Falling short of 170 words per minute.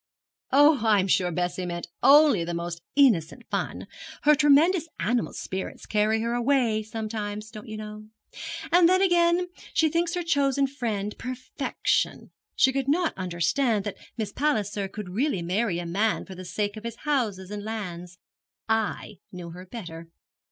Yes: average, 160 wpm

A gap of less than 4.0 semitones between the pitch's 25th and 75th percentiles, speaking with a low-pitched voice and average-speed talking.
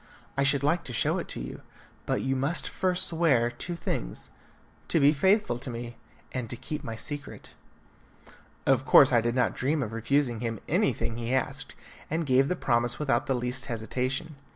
Yes: average, 3.6 semitones; low, 130 Hz; average, 185 wpm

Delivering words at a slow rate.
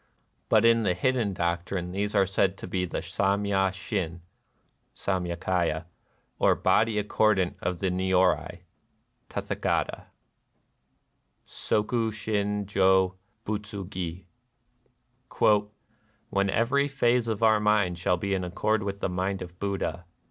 Yes: slow, 130 wpm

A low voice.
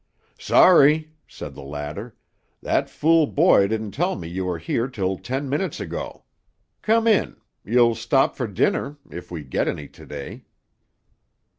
Yes: low, 115 Hz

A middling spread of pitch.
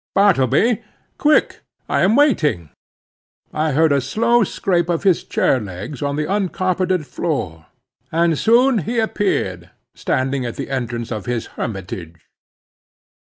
No: wide, 8.5 semitones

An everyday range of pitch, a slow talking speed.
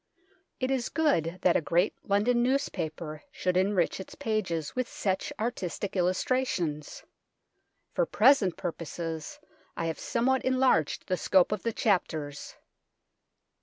No: wide, 6.7 semitones; slow, 125 wpm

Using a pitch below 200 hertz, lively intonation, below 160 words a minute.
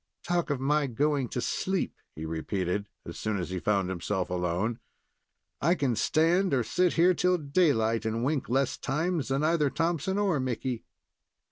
No: low, 135 Hz; wide, 7.2 semitones; average, 165 wpm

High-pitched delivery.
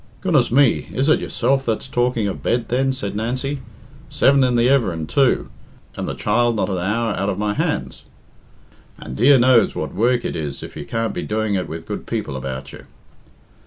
No: low, 115 Hz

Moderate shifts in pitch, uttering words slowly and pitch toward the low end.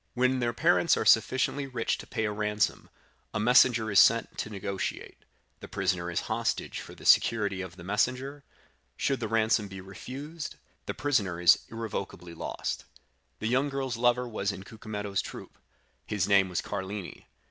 No: average, 4.1 semitones; average, 165 wpm; low, 110 Hz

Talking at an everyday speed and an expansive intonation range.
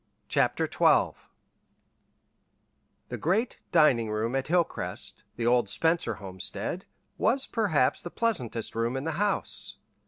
No: slow, 120 wpm; wide, 7.5 semitones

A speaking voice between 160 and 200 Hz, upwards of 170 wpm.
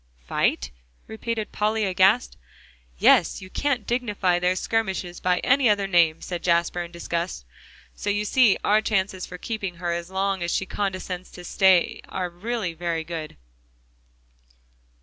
No: medium, 185 Hz; average, 150 wpm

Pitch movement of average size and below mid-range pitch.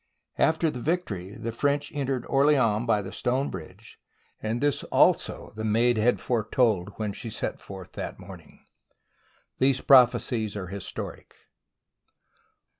Yes: average, 4.4 semitones; low, 115 Hz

